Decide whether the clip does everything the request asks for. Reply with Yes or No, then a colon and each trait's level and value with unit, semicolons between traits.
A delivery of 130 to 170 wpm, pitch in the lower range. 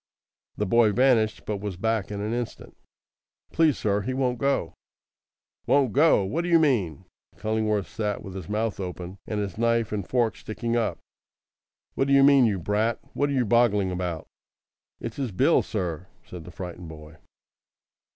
Yes: average, 165 wpm; low, 110 Hz